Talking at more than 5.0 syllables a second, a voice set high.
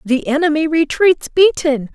No: 4.4 syllables/s; very high, 305 Hz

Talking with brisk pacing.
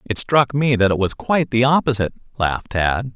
Yes: fast, 210 wpm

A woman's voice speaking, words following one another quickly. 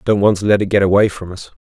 No: male; fast, 335 wpm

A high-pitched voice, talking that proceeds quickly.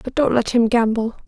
Yes: high, 235 Hz; fast, 235 wpm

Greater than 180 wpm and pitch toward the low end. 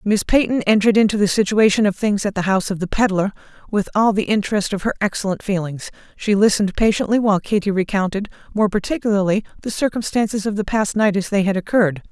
No: average, 200 wpm; high, 205 Hz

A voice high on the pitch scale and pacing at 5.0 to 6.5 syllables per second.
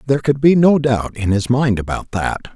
No: low, 125 Hz; 5.1 syllables/s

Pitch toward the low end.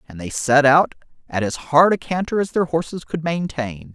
No: medium, 150 Hz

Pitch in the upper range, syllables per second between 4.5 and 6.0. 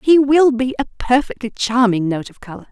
Yes: high, 240 Hz; 5.5 syllables/s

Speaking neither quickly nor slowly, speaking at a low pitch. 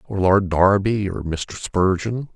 Yes: average, 155 wpm; very low, 95 Hz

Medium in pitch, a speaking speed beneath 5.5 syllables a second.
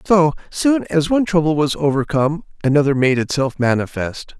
Yes: medium, 150 Hz; 5.3 syllables/s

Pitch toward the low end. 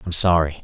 Yes: very low, 85 Hz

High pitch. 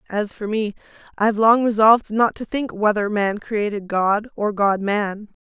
Yes: high, 210 Hz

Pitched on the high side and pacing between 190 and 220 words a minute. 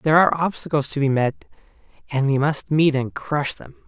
No: medium, 145 Hz; average, 200 wpm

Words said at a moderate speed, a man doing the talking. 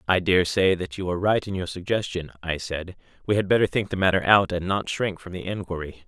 No: fast, 245 wpm; male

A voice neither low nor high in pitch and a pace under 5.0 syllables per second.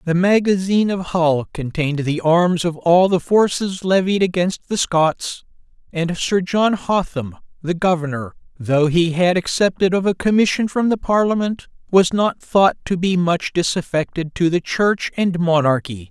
Yes: medium, 175 Hz; 4.5 syllables/s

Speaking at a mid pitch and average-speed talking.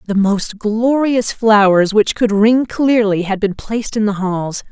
No: high, 215 Hz; average, 180 wpm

